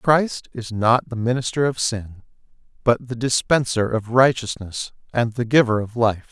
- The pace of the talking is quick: No, average, 160 wpm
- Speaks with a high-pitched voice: No, low, 120 Hz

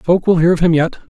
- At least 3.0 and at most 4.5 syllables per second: No, 5.9 syllables/s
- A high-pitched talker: No, medium, 170 Hz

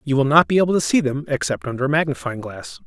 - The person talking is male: Yes, male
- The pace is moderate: No, fast, 270 wpm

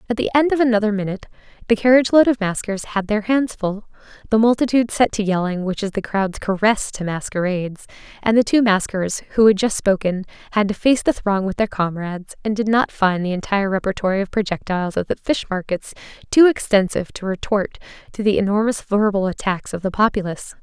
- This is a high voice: Yes, high, 205 Hz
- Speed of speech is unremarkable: Yes, average, 195 wpm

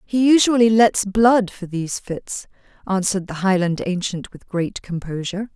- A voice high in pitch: Yes, high, 195 Hz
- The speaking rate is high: No, average, 150 wpm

